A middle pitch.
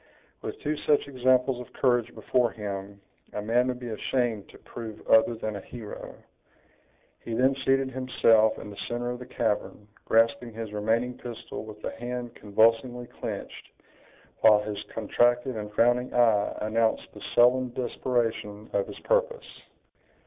No: low, 120 Hz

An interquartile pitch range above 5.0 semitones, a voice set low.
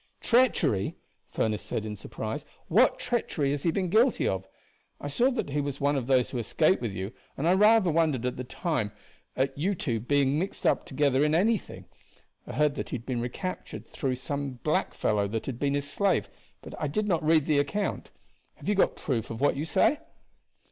No: wide, 5.6 semitones; medium, 145 Hz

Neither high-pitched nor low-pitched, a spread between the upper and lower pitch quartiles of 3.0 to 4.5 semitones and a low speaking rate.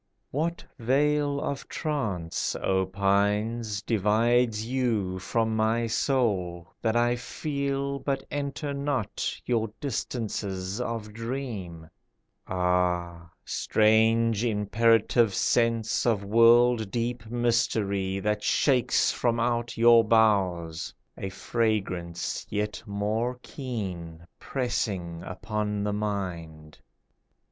No: low, 110 Hz; average, 3.7 semitones; slow, 95 wpm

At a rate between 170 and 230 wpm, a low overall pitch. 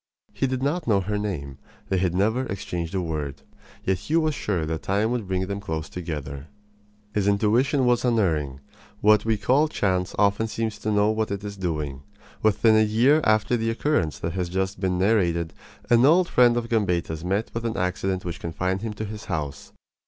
Yes: average, 195 wpm; low, 100 Hz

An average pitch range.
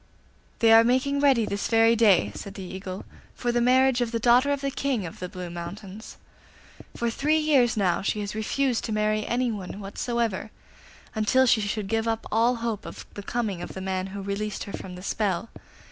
Yes: average, 3.5 semitones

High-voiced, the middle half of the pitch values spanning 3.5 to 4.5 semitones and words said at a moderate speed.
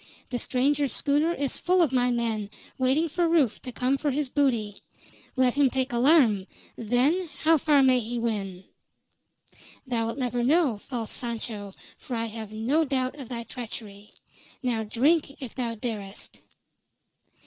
Yes: very high, 250 Hz; average, 3.9 semitones; average, 150 wpm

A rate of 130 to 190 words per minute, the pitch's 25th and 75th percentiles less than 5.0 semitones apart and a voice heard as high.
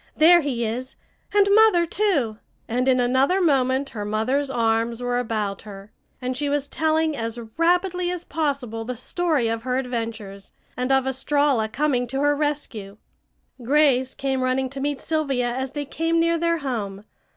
Yes: average, 165 wpm; average, 4.4 semitones; very high, 265 Hz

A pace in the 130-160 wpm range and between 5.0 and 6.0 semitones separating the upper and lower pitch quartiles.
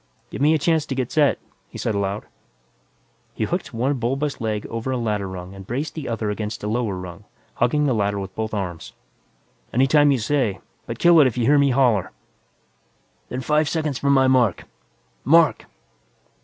No: average, 190 wpm; wide, 5.4 semitones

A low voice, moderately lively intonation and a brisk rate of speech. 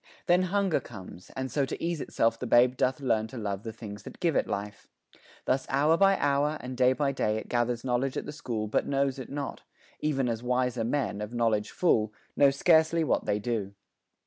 Yes: low, 125 Hz; average, 4.3 semitones; fast, 210 wpm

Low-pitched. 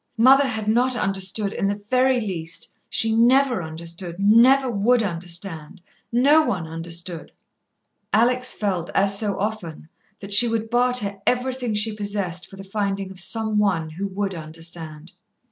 No: high, 200 Hz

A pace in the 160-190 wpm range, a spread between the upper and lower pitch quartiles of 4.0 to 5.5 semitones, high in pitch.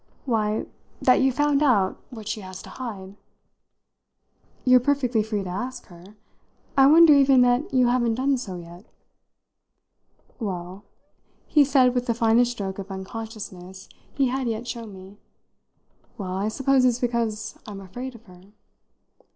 No: average, 150 wpm; average, 4.5 semitones; high, 230 Hz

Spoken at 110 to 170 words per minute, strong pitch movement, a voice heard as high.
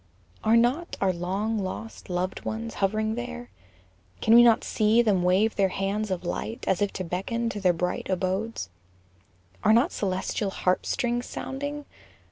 No: average, 160 wpm; average, 3.8 semitones; high, 215 Hz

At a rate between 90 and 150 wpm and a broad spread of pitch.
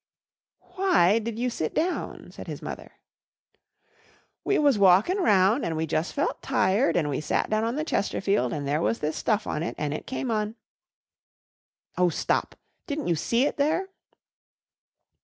No: average, 170 wpm; wide, 8.4 semitones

